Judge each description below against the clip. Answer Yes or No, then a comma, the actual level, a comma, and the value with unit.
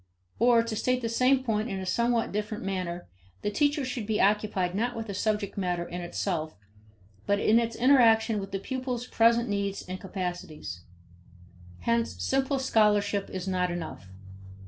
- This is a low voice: No, high, 210 Hz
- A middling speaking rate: Yes, average, 160 wpm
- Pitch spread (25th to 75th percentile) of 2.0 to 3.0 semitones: No, average, 3.8 semitones